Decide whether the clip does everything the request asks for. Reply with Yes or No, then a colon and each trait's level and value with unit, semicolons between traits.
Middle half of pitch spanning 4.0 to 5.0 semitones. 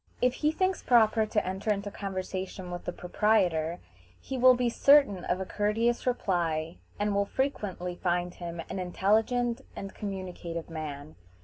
Yes: average, 4.5 semitones